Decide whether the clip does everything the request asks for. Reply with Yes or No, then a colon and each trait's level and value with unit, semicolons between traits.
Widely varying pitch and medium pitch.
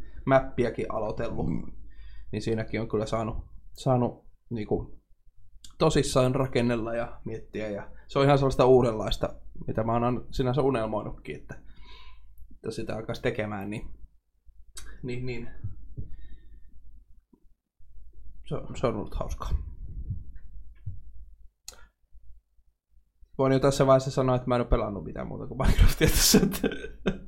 No: wide, 7.2 semitones; low, 110 Hz